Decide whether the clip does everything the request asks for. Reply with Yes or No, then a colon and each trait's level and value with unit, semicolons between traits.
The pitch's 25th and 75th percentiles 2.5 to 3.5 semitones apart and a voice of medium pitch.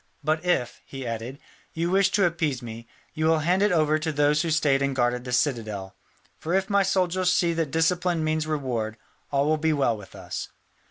No: average, 4.8 semitones; medium, 155 Hz